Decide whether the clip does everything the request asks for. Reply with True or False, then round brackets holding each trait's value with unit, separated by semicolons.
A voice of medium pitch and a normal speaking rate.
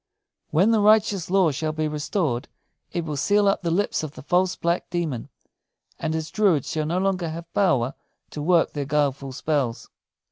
True (160 Hz; 180 wpm)